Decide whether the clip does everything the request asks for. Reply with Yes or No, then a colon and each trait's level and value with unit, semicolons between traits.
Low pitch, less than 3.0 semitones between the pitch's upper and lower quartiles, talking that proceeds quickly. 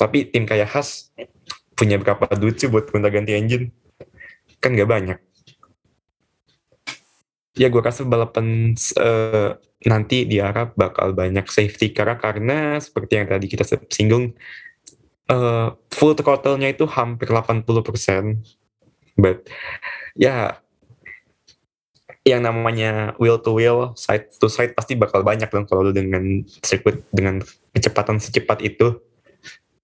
No: low, 110 Hz; narrow, 2.5 semitones; average, 125 wpm